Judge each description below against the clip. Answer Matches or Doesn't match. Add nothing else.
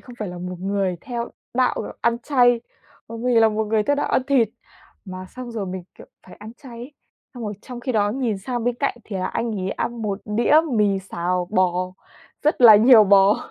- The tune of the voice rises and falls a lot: Doesn't match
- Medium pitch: Doesn't match